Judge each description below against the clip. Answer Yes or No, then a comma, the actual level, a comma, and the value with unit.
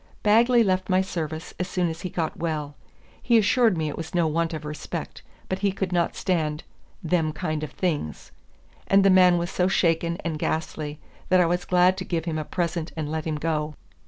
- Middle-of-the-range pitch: Yes, medium, 170 Hz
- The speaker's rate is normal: No, fast, 210 wpm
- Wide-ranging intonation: No, average, 2.9 semitones